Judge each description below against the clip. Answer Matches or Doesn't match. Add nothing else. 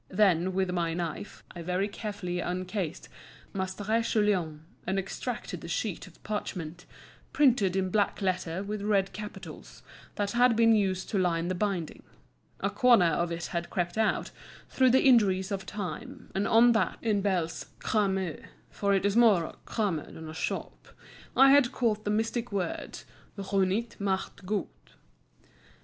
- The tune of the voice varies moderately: Matches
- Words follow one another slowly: Doesn't match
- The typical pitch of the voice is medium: Doesn't match